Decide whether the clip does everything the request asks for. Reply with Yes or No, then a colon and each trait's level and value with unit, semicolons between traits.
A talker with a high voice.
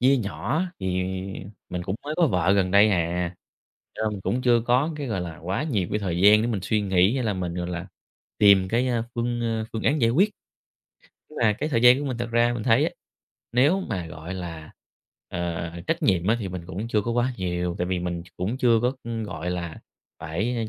No: low, 105 Hz